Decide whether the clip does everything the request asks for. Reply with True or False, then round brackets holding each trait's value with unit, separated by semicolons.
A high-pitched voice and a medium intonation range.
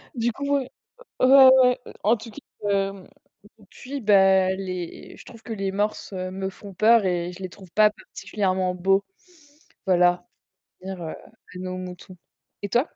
True (195 Hz; 3.0 semitones)